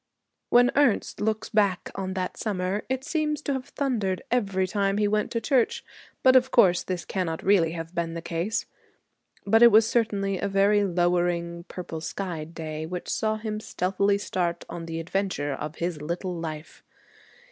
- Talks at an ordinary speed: Yes, average, 170 wpm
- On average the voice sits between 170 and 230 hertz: Yes, high, 190 Hz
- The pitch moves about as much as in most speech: Yes, average, 4.0 semitones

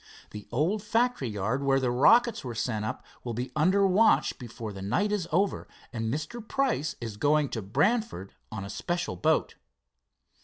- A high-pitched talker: No, medium, 140 Hz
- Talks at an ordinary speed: Yes, average, 170 wpm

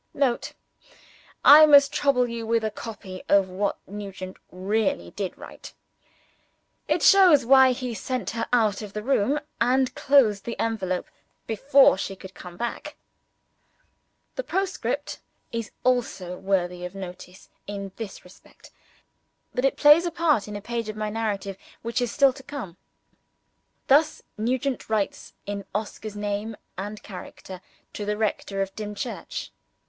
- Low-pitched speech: No, high, 215 Hz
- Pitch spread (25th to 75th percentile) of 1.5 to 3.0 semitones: No, average, 4.5 semitones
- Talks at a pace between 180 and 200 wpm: No, average, 145 wpm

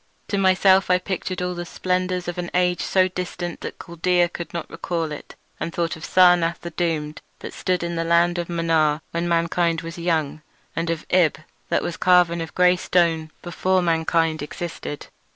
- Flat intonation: Yes, narrow, 1.4 semitones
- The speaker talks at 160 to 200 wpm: Yes, average, 185 wpm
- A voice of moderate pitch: Yes, medium, 170 Hz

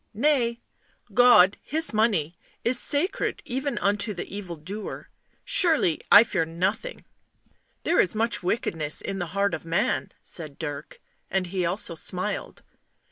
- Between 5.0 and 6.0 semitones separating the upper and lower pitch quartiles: Yes, wide, 5.5 semitones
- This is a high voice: Yes, high, 200 Hz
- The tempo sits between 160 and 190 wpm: No, slow, 135 wpm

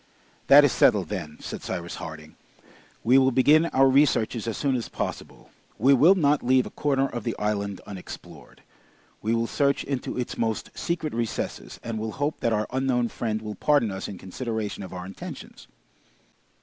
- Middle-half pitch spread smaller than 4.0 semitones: No, average, 4.4 semitones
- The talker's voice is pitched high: No, low, 115 Hz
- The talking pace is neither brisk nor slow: Yes, average, 175 wpm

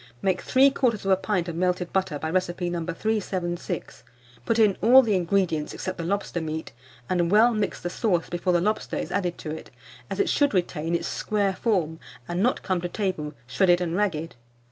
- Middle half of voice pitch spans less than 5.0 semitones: Yes, average, 3.2 semitones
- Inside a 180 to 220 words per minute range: Yes, average, 190 wpm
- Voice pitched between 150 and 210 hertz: Yes, medium, 185 Hz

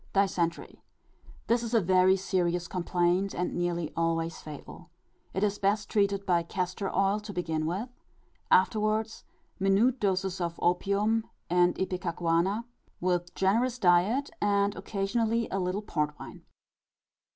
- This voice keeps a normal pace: No, slow, 130 wpm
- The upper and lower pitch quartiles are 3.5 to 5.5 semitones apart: No, average, 2.7 semitones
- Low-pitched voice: No, high, 190 Hz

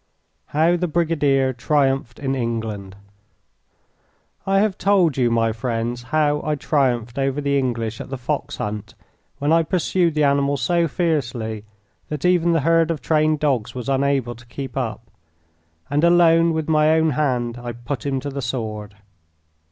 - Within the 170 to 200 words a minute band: No, average, 160 wpm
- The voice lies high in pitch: No, medium, 140 Hz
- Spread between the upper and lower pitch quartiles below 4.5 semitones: No, average, 4.8 semitones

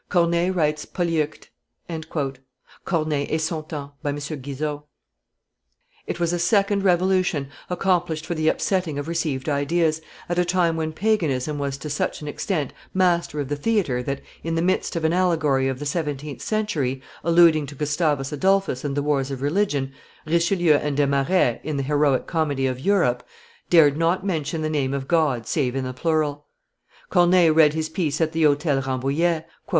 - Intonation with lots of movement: No, average, 3.3 semitones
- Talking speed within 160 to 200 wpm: Yes, average, 170 wpm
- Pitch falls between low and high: Yes, medium, 155 Hz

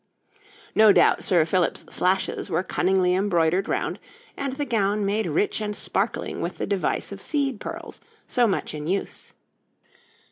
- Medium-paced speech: Yes, average, 150 wpm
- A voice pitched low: No, high, 195 Hz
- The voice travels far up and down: No, average, 3.2 semitones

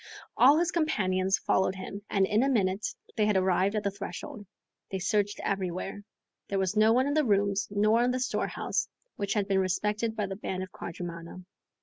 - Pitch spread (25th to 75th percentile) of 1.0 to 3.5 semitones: Yes, narrow, 2.4 semitones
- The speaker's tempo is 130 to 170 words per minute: No, average, 195 wpm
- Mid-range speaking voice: No, high, 200 Hz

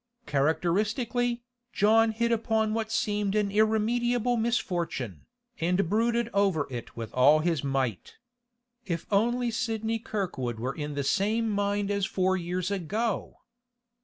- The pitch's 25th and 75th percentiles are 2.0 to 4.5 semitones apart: No, average, 5.3 semitones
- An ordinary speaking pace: No, slow, 130 wpm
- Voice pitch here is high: Yes, high, 205 Hz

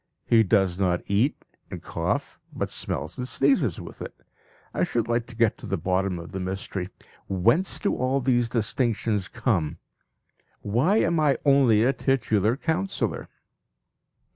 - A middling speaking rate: Yes, average, 150 wpm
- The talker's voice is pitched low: Yes, low, 115 Hz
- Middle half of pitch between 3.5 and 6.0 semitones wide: Yes, wide, 5.6 semitones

